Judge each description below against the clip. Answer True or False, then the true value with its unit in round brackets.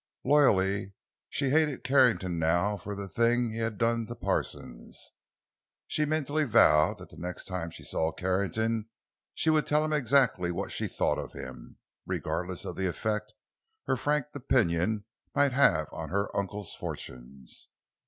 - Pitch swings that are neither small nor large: False (6.5 semitones)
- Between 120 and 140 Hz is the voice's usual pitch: False (105 Hz)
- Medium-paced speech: True (155 wpm)